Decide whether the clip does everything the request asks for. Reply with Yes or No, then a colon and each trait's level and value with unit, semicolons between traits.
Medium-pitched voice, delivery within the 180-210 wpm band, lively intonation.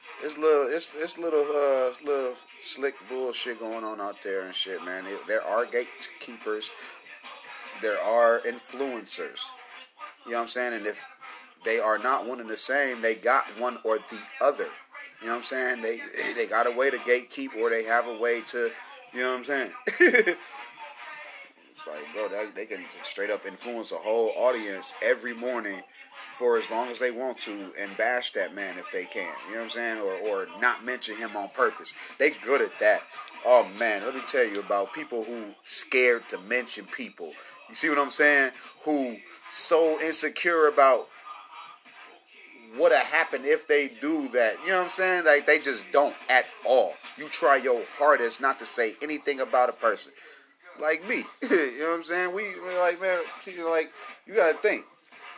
Yes: medium, 145 Hz; average, 190 wpm; wide, 8.7 semitones